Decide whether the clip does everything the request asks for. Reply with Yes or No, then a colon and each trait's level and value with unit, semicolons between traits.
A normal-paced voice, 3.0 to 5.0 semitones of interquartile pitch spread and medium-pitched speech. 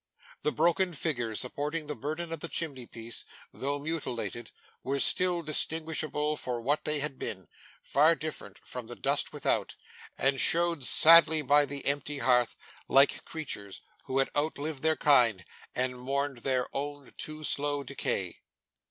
Yes: average, 150 wpm; average, 3.5 semitones; medium, 145 Hz